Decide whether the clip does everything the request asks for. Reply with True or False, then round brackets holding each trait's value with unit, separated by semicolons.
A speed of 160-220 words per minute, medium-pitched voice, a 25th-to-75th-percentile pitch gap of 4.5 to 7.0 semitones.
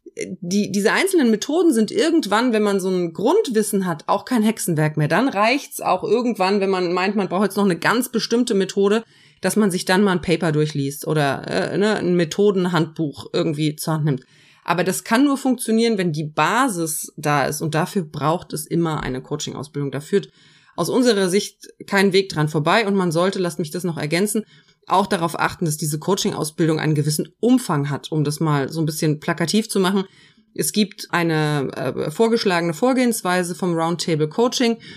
True (190 wpm; 180 Hz; 5.1 semitones)